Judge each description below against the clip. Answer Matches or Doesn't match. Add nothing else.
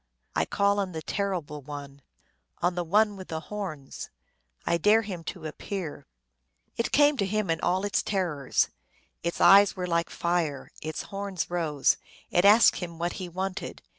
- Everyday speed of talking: Matches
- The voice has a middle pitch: Matches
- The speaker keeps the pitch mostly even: Doesn't match